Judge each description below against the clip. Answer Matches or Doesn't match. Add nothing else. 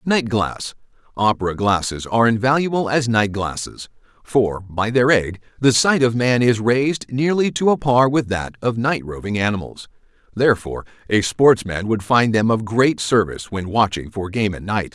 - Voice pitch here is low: Matches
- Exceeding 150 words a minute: Matches